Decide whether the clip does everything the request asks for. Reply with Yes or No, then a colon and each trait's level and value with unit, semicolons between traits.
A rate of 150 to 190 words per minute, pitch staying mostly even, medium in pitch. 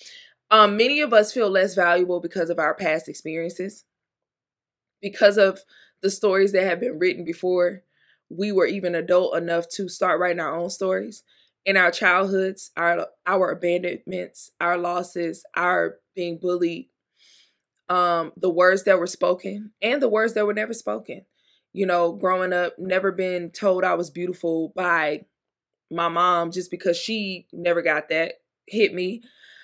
Yes: average, 155 wpm; narrow, 2.1 semitones; medium, 180 Hz